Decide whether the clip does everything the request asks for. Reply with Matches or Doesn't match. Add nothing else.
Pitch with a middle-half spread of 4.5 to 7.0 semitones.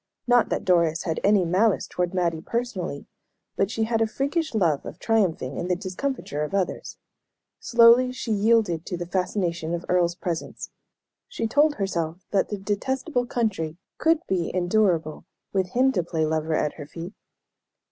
Matches